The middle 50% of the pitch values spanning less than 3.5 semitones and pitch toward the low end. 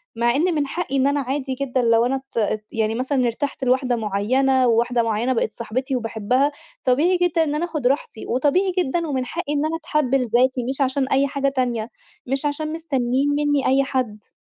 No: average, 3.1 semitones; very high, 265 Hz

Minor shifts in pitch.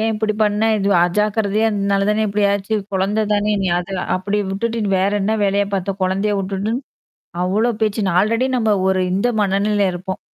Yes: narrow, 1.7 semitones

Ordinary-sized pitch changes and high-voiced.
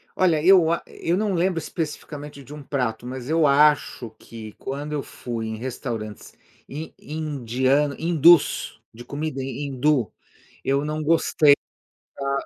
No: average, 3.5 semitones; medium, 145 Hz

